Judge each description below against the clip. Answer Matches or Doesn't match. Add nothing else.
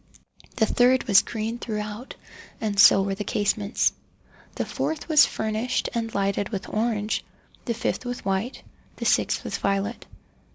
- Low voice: Doesn't match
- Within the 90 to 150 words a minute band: Matches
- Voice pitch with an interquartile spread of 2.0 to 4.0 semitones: Matches